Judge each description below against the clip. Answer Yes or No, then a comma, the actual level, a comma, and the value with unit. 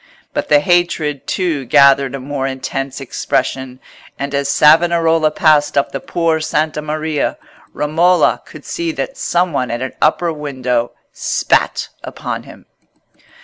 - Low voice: No, medium, 150 Hz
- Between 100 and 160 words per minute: Yes, average, 140 wpm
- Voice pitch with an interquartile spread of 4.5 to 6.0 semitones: No, average, 3.1 semitones